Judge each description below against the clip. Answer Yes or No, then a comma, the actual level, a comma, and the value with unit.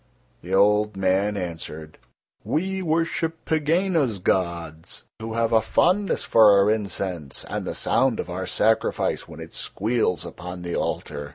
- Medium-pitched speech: No, low, 105 Hz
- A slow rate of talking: No, average, 145 wpm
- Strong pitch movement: Yes, wide, 6.8 semitones